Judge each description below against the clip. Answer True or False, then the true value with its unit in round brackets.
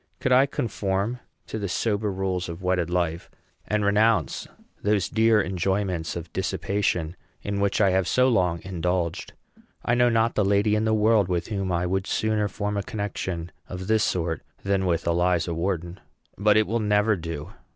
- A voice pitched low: True (95 Hz)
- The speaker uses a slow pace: False (175 wpm)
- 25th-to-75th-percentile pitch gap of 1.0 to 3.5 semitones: True (3.2 semitones)